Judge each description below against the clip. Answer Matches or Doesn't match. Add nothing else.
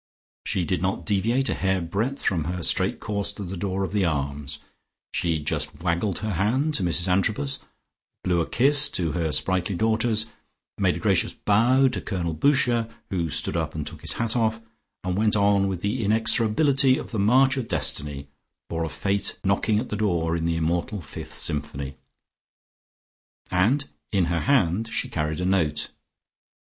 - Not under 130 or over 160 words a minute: Doesn't match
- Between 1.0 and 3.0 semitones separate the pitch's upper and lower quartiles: Doesn't match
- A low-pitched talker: Matches